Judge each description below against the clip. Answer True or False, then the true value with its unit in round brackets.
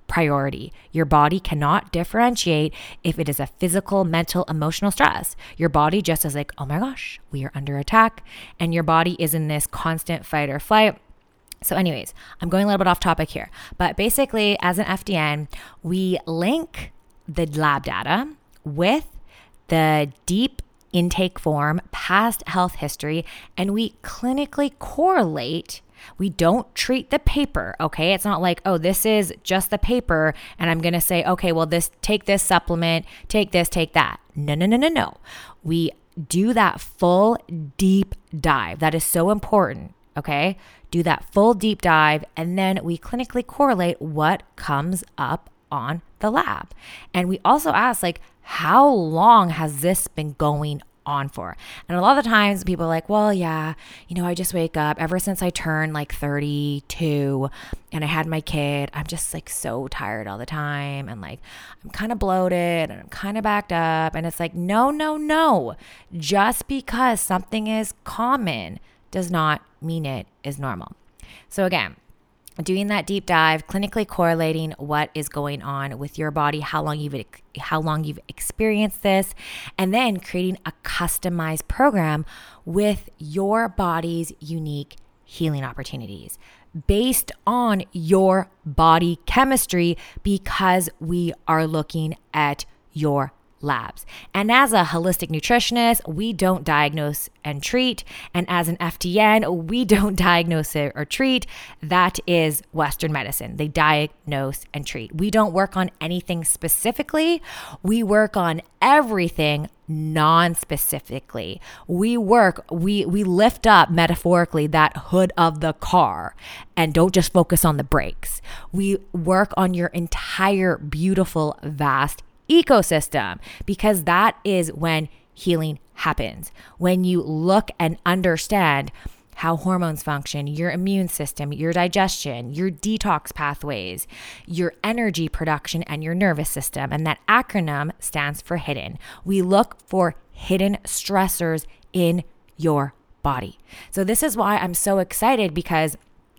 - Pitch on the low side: False (170 Hz)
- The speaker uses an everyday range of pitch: True (4.3 semitones)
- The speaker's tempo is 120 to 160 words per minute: True (150 wpm)